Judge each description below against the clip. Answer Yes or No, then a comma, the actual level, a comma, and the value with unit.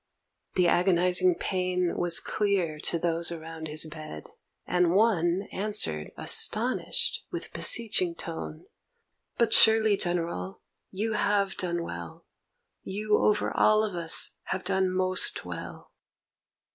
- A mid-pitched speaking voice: Yes, medium, 180 Hz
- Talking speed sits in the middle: No, slow, 120 wpm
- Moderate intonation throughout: Yes, average, 3.4 semitones